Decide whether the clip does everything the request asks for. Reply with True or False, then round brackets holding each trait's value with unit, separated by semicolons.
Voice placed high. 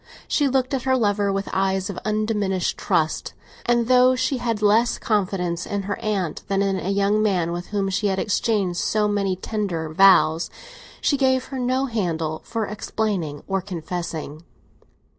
True (200 Hz)